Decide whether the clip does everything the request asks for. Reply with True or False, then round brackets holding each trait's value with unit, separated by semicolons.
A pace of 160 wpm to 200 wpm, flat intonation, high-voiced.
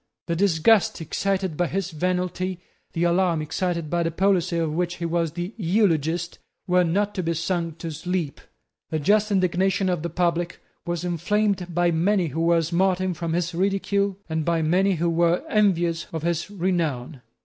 False (170 wpm; 2.1 semitones; 175 Hz)